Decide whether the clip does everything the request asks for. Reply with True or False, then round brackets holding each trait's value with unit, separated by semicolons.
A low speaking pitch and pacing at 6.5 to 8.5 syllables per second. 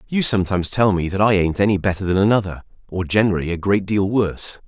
True (100 Hz; 6.7 syllables/s)